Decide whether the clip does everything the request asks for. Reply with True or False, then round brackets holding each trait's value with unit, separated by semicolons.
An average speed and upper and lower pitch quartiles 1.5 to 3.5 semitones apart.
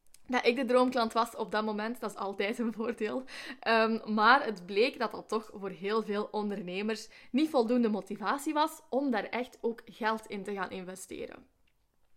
True (185 wpm; 2.9 semitones)